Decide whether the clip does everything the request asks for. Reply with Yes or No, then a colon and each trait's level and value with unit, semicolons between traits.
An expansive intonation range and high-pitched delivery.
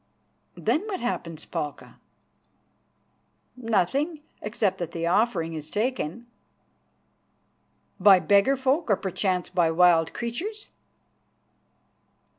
Yes: wide, 6.9 semitones; high, 200 Hz